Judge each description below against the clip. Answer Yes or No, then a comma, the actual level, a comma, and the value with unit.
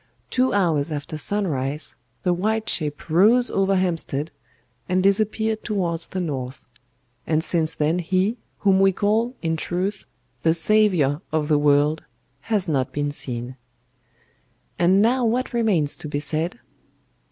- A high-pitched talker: No, medium, 175 Hz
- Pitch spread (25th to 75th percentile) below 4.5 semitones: No, average, 5.3 semitones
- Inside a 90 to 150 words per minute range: Yes, average, 140 wpm